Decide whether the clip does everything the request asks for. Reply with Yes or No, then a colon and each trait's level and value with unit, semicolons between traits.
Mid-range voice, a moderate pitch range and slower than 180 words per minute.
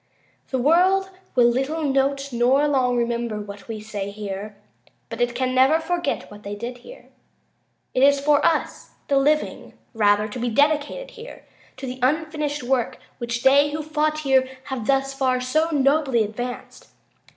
No: very high, 265 Hz; average, 3.9 semitones; average, 160 wpm